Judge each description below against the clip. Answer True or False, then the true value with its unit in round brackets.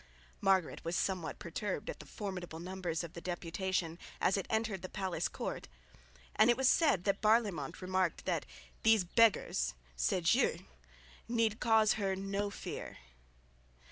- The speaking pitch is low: False (190 Hz)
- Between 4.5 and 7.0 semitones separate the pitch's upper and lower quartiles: False (3.6 semitones)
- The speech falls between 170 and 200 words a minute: False (145 wpm)